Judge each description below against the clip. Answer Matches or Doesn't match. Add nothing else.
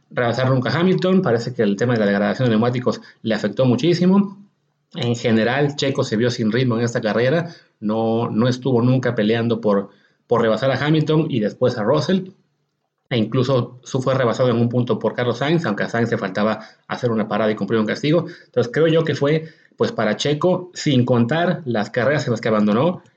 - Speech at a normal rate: Doesn't match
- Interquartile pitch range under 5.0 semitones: Doesn't match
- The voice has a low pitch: Matches